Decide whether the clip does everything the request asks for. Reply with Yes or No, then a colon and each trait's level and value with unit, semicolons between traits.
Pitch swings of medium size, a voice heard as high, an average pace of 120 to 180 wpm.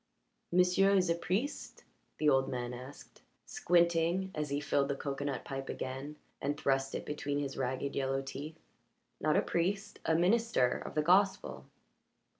No: average, 4.7 semitones; medium, 150 Hz; average, 155 wpm